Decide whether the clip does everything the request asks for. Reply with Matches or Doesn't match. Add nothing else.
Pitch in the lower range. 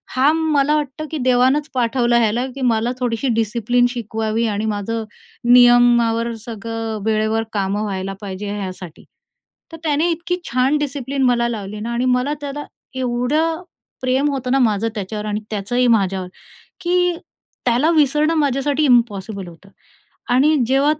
Doesn't match